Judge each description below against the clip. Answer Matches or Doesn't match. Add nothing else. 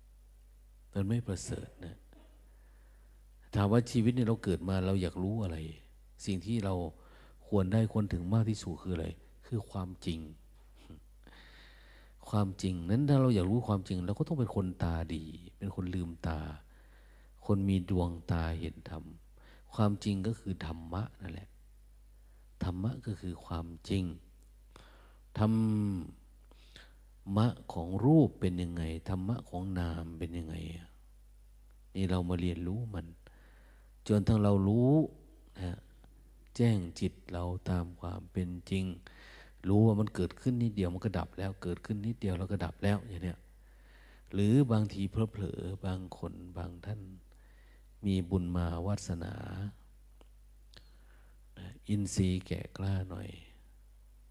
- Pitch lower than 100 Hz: Matches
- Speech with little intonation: Doesn't match